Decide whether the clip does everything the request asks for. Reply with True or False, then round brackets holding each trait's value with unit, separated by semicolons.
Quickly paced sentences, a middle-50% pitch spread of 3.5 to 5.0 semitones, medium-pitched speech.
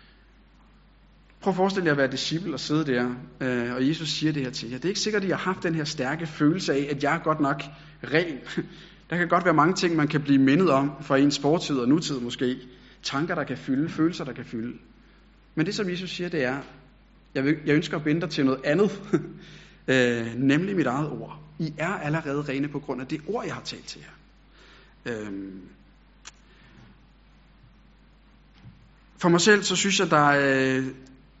False (200 wpm; 4.2 semitones; 150 Hz)